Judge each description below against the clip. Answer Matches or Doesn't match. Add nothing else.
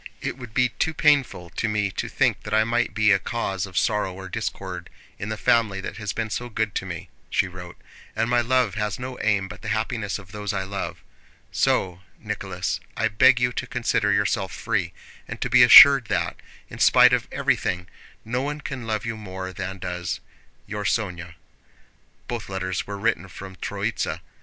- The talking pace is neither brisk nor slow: Matches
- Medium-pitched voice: Doesn't match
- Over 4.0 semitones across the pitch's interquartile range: Doesn't match